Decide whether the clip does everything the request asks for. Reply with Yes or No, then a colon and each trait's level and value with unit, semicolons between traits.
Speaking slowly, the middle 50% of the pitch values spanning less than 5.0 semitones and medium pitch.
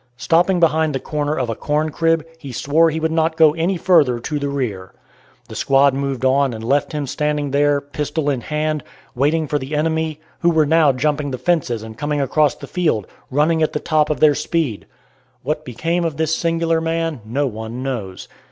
No: average, 200 wpm; average, 2.9 semitones; medium, 150 Hz